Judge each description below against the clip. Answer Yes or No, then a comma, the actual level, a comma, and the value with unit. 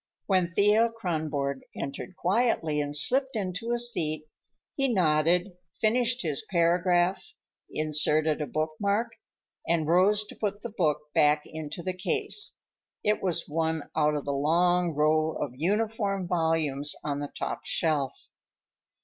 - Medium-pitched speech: Yes, medium, 170 Hz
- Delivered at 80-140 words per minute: Yes, slow, 135 wpm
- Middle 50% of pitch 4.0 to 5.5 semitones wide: Yes, average, 5.2 semitones